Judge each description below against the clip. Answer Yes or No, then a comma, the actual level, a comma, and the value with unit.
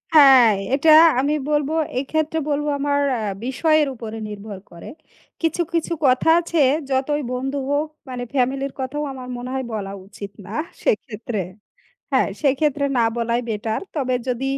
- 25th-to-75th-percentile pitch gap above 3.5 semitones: Yes, average, 3.9 semitones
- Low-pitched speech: No, very high, 265 Hz